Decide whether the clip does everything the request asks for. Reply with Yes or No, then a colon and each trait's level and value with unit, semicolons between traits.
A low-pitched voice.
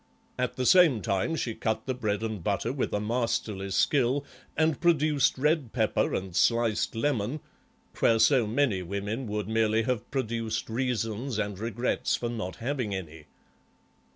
Yes: low, 115 Hz